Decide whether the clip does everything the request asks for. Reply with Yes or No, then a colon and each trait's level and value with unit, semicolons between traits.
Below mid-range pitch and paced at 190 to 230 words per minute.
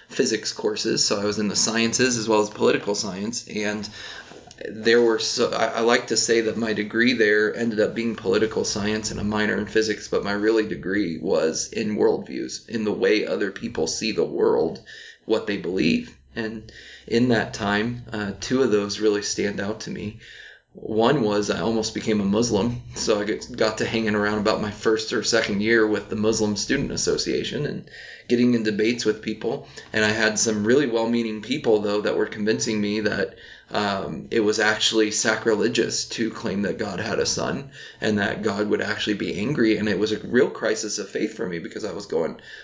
Yes: low, 110 Hz; average, 200 wpm